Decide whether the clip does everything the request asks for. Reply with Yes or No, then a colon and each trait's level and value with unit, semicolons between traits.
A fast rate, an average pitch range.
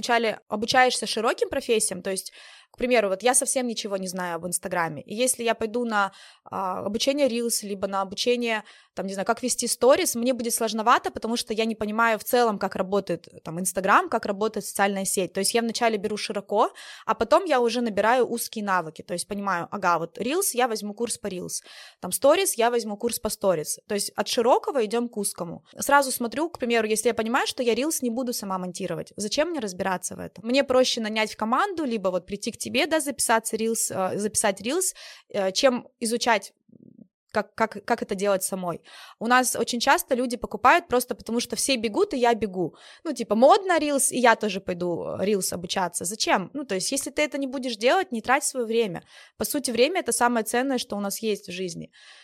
Yes: fast, 210 wpm; average, 3.8 semitones